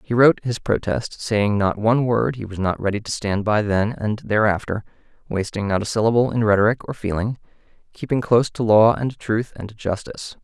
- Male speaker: Yes, male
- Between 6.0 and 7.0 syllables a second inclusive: No, 5.4 syllables/s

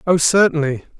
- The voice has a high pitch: No, medium, 160 Hz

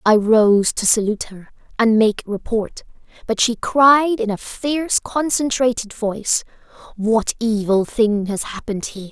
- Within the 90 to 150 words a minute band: Yes, average, 140 wpm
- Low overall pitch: No, high, 225 Hz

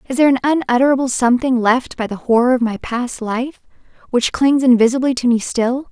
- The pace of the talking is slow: No, average, 195 wpm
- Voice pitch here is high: Yes, very high, 250 Hz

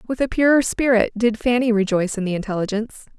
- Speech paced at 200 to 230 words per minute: No, average, 190 wpm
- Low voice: No, high, 225 Hz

